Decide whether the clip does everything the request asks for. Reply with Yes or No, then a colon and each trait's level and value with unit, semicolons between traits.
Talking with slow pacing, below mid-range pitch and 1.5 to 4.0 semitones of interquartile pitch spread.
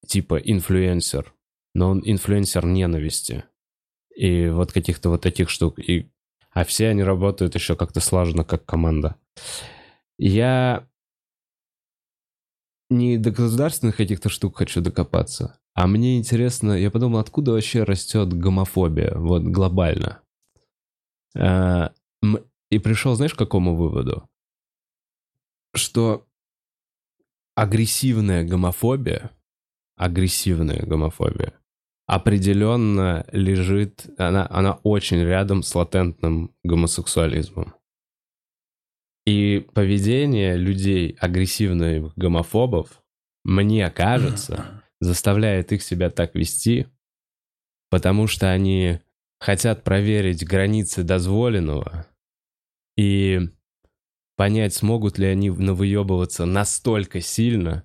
Yes: slow, 90 wpm; very low, 95 Hz; average, 3.5 semitones